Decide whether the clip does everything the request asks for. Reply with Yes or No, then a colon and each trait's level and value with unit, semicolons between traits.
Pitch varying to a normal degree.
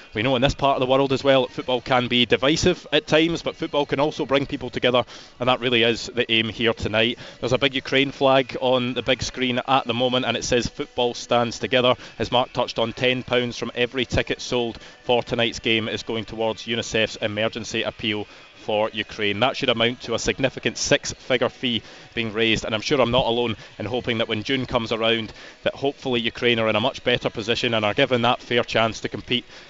No: narrow, 2.3 semitones